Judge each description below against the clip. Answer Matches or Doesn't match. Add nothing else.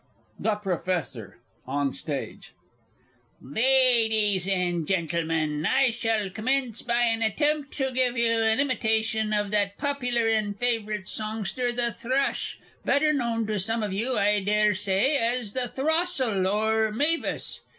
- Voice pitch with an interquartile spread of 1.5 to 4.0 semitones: Matches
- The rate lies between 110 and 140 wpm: Matches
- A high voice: Matches